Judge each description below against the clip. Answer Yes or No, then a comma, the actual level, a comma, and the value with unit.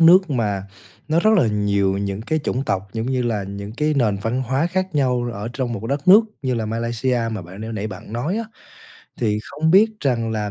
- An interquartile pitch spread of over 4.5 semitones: Yes, average, 5.3 semitones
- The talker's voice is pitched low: Yes, low, 120 Hz